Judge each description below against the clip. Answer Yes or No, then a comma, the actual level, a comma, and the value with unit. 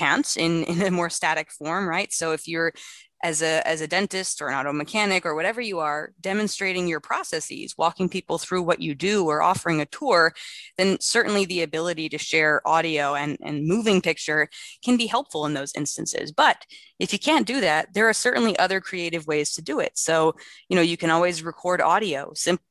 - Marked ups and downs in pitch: No, average, 3.2 semitones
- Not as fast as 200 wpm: No, fast, 205 wpm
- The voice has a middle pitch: Yes, medium, 170 Hz